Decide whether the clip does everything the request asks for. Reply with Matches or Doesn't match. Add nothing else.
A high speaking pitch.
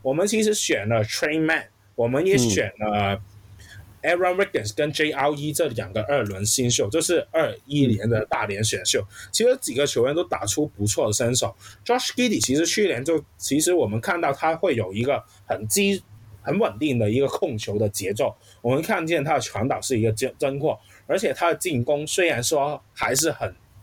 Doesn't match